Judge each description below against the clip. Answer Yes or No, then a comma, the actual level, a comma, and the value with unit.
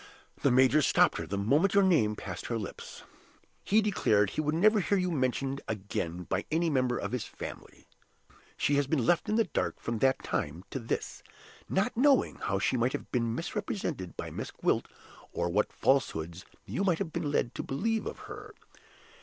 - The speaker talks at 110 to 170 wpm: No, average, 190 wpm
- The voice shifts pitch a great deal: Yes, wide, 8.9 semitones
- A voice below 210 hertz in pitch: Yes, medium, 140 Hz